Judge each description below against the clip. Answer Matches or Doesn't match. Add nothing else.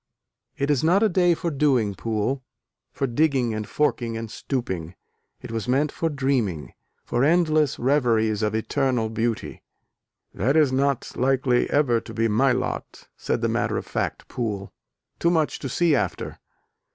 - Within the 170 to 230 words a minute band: Doesn't match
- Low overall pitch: Matches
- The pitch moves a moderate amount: Matches